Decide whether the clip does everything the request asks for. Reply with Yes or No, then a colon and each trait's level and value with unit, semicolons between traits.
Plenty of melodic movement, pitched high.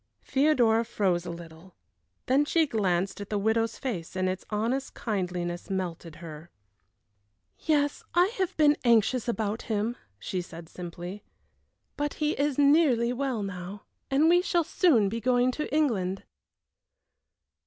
Yes: wide, 7.1 semitones; high, 220 Hz